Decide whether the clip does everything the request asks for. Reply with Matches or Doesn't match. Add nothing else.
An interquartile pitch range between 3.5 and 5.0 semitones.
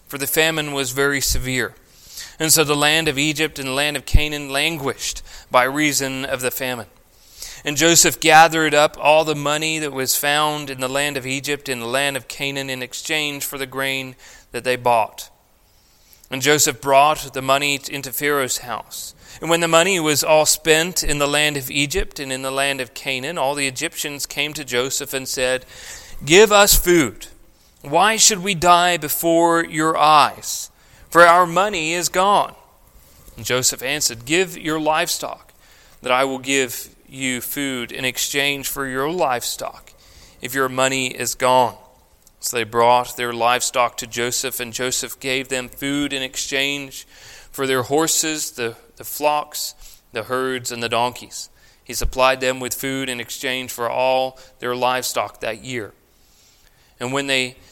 Doesn't match